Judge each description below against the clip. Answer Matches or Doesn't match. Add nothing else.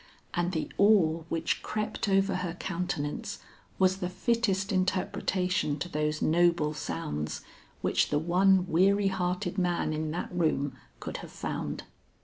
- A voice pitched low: Doesn't match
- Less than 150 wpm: Matches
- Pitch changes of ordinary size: Matches